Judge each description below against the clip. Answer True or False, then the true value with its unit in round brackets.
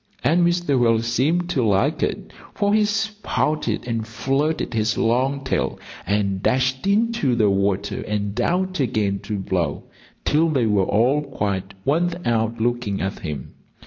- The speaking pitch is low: True (120 Hz)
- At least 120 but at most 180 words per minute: True (150 wpm)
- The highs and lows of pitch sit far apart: True (7.1 semitones)